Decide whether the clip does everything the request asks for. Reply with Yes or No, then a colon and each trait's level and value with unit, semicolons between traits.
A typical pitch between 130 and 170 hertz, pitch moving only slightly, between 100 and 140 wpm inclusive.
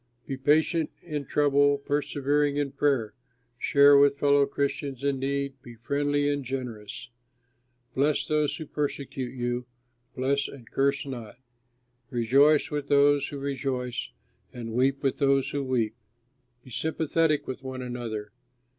Yes: medium, 140 Hz; narrow, 2.1 semitones; slow, 135 wpm